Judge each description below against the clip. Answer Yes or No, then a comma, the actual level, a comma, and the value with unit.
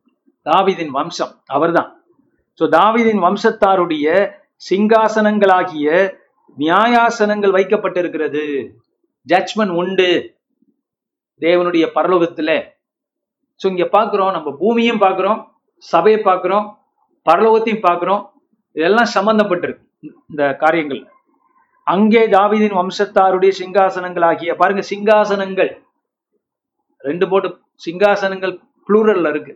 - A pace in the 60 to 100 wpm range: Yes, average, 80 wpm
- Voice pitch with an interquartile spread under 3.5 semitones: No, average, 3.9 semitones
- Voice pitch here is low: No, high, 195 Hz